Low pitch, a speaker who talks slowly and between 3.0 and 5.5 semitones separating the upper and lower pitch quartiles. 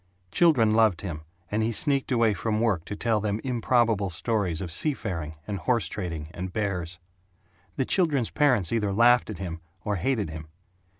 No: low, 105 Hz; average, 175 wpm; average, 4.6 semitones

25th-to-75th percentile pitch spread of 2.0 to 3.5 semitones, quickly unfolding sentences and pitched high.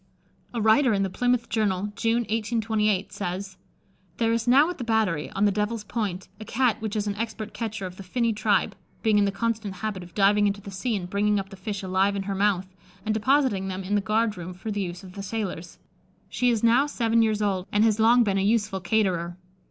Yes: narrow, 2.6 semitones; fast, 230 wpm; high, 210 Hz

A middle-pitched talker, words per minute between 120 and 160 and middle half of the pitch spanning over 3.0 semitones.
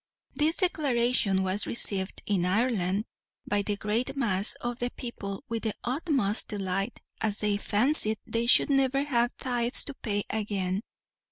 No: high, 220 Hz; average, 150 wpm; average, 3.6 semitones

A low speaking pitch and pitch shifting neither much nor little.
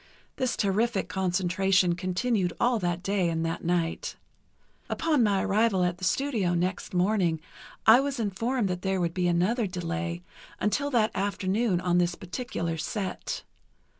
No: medium, 185 Hz; average, 3.8 semitones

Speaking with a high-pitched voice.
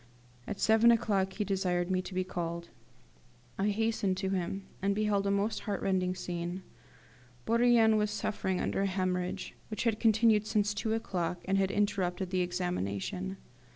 Yes: high, 195 Hz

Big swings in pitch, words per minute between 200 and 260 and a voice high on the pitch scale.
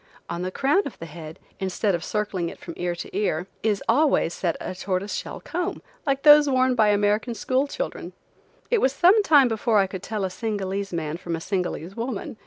Yes: wide, 6.1 semitones; fast, 205 wpm; high, 205 Hz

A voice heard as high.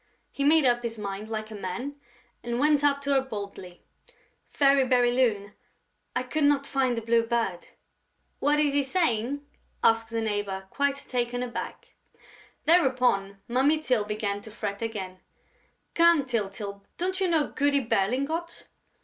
Yes: high, 245 Hz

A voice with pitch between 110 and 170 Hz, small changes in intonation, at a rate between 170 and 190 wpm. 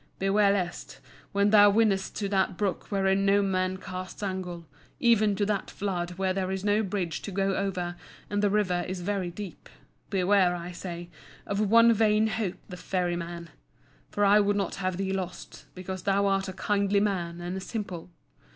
No: high, 195 Hz; narrow, 2.0 semitones; average, 180 wpm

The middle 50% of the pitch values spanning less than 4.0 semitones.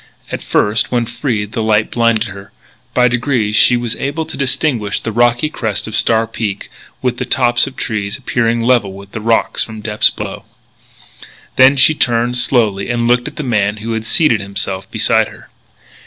Yes: narrow, 2.6 semitones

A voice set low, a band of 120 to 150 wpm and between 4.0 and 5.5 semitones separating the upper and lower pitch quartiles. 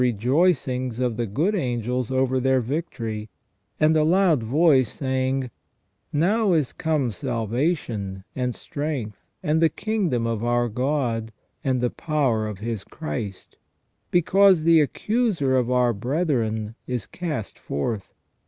Yes: low, 130 Hz; slow, 135 wpm; average, 5.2 semitones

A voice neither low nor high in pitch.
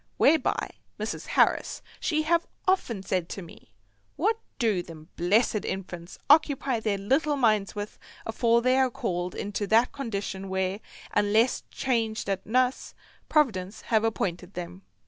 No: high, 220 Hz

